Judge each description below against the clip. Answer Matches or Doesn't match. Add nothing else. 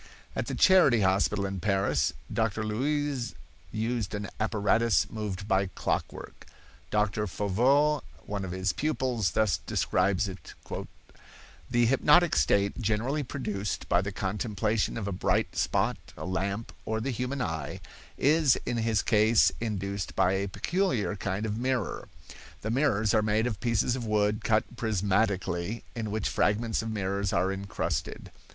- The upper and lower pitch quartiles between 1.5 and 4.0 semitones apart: Matches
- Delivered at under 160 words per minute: Matches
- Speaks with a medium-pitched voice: Doesn't match